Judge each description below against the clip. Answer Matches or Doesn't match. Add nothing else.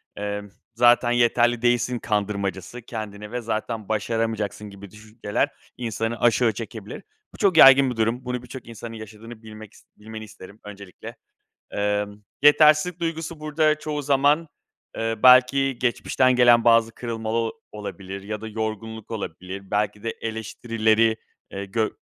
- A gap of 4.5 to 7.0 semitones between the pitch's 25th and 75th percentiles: Doesn't match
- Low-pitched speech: Matches